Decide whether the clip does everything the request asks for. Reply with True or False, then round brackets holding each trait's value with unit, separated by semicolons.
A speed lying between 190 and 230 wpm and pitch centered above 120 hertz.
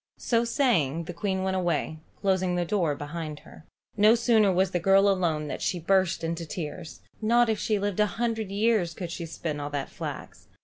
True (200 wpm; 185 Hz)